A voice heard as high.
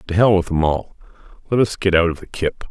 No: very low, 90 Hz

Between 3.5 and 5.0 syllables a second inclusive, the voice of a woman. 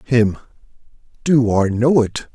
No: 3.7 syllables/s; male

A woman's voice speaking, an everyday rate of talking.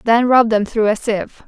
No: female; fast, 245 wpm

